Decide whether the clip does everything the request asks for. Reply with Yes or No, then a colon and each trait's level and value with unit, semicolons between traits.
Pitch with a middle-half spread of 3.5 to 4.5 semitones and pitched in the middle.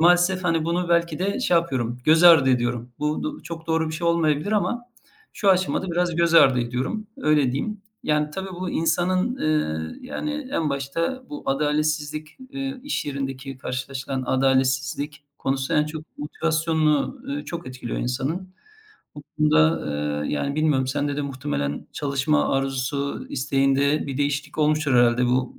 Yes: average, 4.2 semitones; medium, 150 Hz